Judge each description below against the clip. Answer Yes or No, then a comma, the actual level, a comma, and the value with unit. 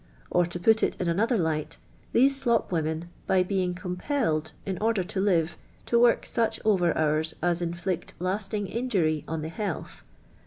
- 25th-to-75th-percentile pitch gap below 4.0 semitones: No, average, 4.3 semitones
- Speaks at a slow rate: No, average, 170 wpm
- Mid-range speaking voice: Yes, medium, 180 Hz